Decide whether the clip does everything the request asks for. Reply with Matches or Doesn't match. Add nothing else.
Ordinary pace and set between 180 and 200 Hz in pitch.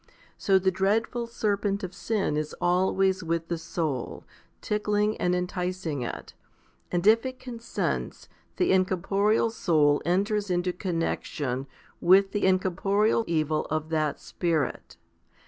Doesn't match